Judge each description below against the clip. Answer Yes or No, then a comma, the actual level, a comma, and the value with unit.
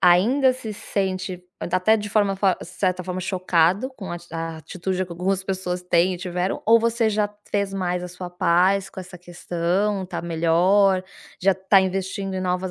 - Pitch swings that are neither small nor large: No, narrow, 1.8 semitones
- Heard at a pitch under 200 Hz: Yes, medium, 185 Hz